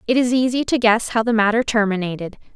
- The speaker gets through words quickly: Yes, fast, 210 wpm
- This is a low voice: No, high, 225 Hz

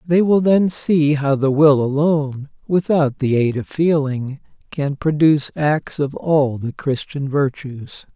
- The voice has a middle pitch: Yes, medium, 145 Hz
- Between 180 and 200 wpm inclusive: No, average, 155 wpm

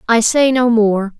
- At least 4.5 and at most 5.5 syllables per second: No, 4.0 syllables/s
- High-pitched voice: Yes, high, 230 Hz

